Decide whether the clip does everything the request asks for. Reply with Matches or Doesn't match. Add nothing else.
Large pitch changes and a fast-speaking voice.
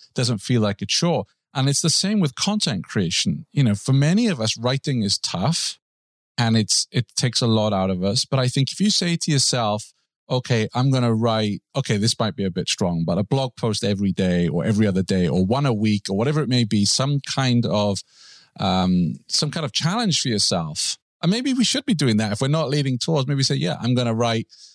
Matches